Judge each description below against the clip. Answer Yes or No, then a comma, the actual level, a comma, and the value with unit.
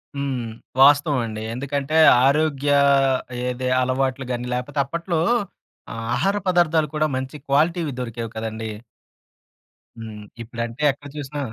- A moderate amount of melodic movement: Yes, average, 3.7 semitones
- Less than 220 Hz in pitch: Yes, low, 135 Hz